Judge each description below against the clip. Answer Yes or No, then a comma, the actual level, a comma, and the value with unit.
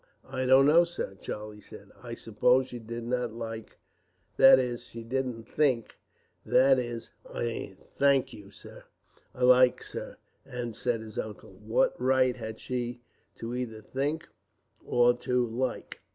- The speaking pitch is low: Yes, low, 125 Hz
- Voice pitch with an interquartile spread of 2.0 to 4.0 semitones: Yes, narrow, 2.4 semitones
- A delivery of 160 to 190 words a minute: No, average, 140 wpm